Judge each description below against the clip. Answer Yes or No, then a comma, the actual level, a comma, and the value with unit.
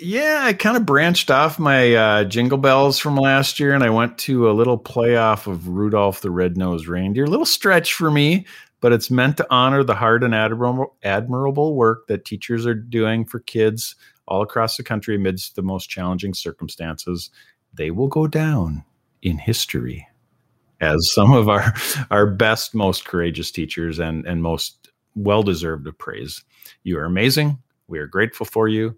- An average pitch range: No, wide, 5.9 semitones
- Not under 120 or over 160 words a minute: No, average, 175 wpm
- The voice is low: Yes, low, 115 Hz